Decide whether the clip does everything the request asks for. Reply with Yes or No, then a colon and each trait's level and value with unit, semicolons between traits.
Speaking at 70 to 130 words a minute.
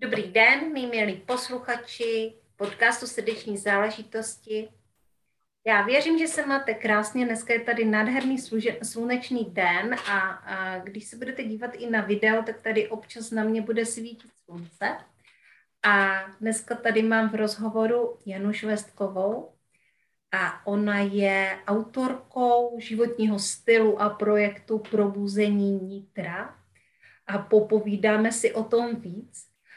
Yes: average, 125 wpm